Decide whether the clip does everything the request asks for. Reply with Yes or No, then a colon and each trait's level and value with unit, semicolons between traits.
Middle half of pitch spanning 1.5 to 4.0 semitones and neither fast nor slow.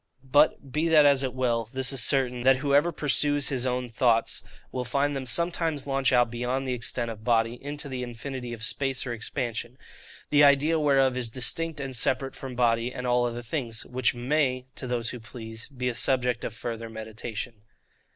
Yes: average, 2.7 semitones; average, 190 wpm